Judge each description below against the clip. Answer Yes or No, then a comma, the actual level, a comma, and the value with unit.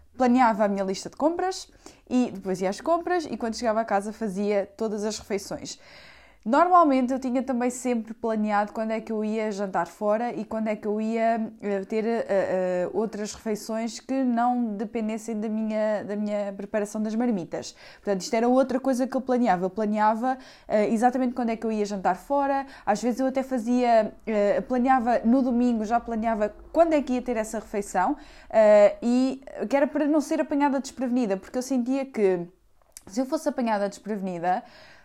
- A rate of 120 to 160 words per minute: No, fast, 185 wpm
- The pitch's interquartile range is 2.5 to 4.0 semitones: Yes, average, 3.7 semitones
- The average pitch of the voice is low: No, high, 225 Hz